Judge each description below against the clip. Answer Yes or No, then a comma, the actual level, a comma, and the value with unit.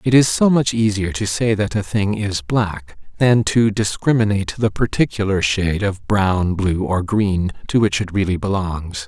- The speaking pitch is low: Yes, low, 100 Hz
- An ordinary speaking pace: Yes, average, 185 wpm